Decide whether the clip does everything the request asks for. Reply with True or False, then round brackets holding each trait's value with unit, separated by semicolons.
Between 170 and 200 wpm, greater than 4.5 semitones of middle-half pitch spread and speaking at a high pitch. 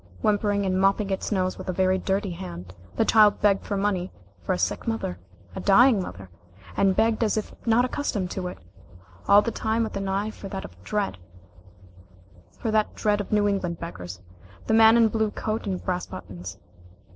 False (180 wpm; 4.2 semitones; 195 Hz)